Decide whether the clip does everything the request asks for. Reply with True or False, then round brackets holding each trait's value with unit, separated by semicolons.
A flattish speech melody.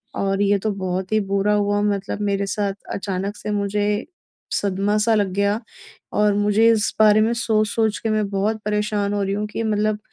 True (1.1 semitones)